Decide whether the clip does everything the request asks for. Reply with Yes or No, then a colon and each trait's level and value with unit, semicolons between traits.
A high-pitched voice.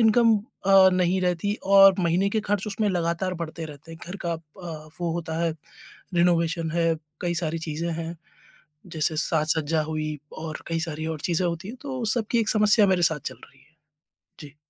No: medium, 170 Hz